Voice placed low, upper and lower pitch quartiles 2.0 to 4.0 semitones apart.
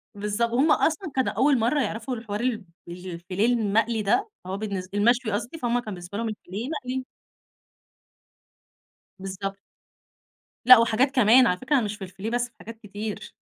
No: high, 225 Hz; average, 3.7 semitones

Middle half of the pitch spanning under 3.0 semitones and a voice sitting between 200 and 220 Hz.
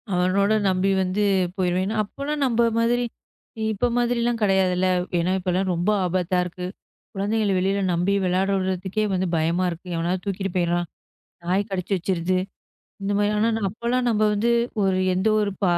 No: narrow, 2.5 semitones; high, 190 Hz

